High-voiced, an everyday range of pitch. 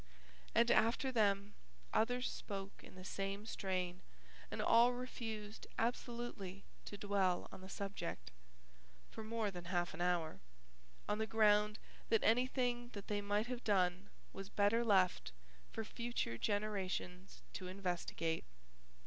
Yes: high, 205 Hz; average, 3.4 semitones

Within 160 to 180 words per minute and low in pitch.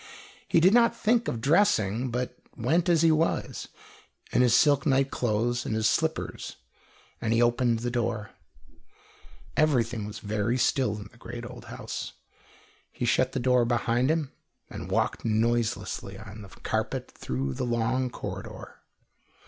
No: average, 150 wpm; low, 120 Hz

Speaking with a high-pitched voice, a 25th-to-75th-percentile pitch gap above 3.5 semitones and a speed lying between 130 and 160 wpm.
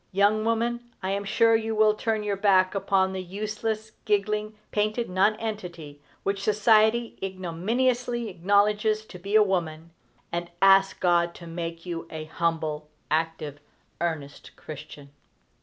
Yes: high, 195 Hz; average, 4.1 semitones; slow, 135 wpm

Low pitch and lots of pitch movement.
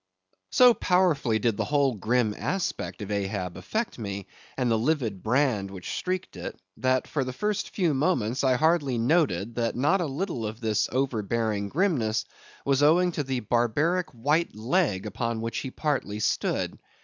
Yes: low, 125 Hz; wide, 6.1 semitones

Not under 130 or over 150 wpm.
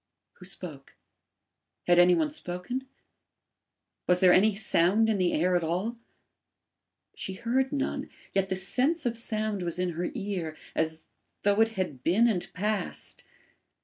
Yes: average, 145 wpm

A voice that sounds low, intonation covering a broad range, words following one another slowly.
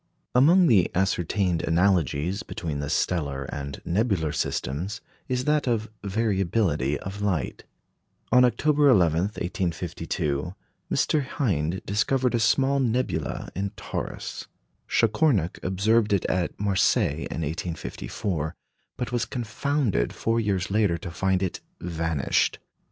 Yes: very low, 95 Hz; wide, 5.7 semitones; slow, 120 wpm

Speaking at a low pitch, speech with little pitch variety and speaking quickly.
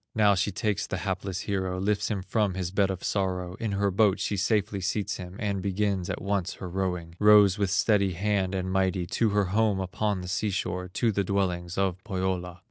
Yes: very low, 95 Hz; narrow, 1.9 semitones; fast, 210 wpm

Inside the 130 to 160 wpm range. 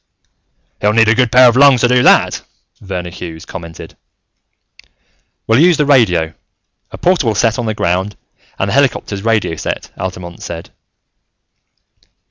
Yes: average, 145 wpm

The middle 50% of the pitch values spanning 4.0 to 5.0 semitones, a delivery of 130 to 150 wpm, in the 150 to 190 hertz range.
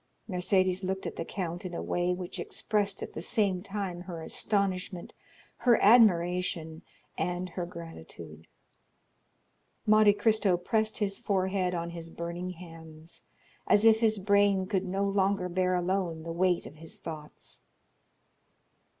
No: average, 2.7 semitones; average, 140 wpm; medium, 185 Hz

